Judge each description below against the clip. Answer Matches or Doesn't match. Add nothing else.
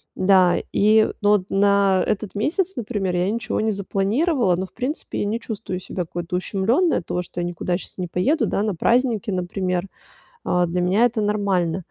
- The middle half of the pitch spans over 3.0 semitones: Matches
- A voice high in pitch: Matches